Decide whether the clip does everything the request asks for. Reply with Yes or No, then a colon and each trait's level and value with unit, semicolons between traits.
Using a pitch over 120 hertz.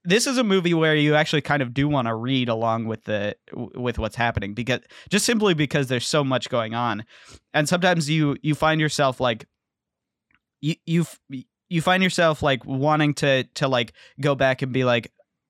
Yes: medium, 140 Hz